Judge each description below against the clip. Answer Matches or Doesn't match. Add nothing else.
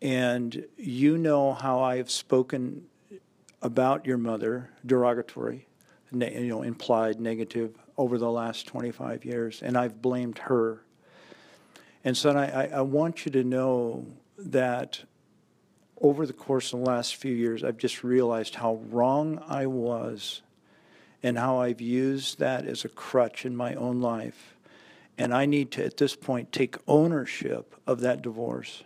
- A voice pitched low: Matches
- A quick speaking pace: Doesn't match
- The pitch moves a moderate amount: Doesn't match